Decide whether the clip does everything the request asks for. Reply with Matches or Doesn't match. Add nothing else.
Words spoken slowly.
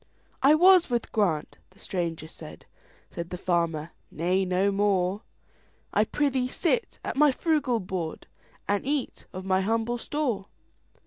Matches